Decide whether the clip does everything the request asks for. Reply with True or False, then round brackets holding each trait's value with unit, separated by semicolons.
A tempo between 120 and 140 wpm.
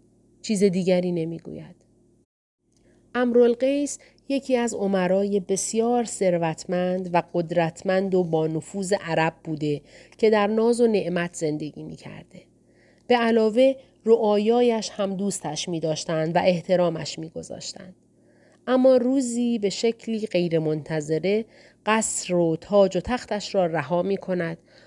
False (105 wpm)